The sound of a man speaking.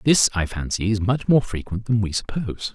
Yes: male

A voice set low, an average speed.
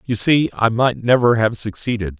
Yes: low, 110 Hz; average, 190 wpm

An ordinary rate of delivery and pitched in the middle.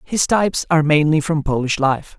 Yes: average, 190 wpm; medium, 155 Hz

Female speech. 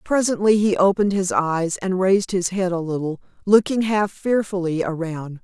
Yes: female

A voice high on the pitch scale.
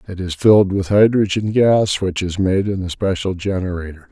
No: very low, 95 Hz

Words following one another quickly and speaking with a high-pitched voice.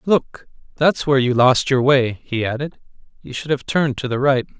No: fast, 210 wpm; low, 135 Hz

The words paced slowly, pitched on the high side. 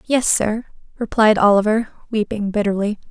Yes: slow, 115 wpm; high, 215 Hz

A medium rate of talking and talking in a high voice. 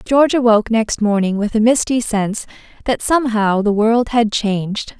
Yes: average, 170 wpm; high, 225 Hz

